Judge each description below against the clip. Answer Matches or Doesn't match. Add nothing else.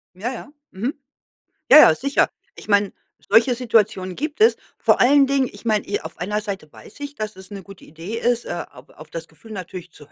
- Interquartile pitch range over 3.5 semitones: Matches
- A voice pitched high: Matches